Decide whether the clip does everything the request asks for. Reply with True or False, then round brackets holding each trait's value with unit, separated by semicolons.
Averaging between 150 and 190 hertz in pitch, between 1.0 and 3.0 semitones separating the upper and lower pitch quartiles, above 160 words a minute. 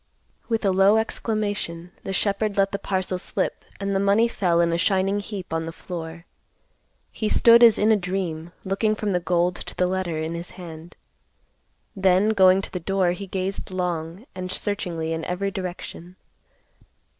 True (185 Hz; 2.4 semitones; 175 wpm)